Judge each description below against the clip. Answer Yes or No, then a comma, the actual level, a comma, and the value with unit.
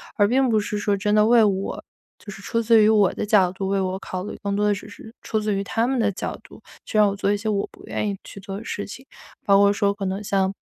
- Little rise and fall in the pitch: Yes, narrow, 1.5 semitones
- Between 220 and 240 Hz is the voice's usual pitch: No, high, 205 Hz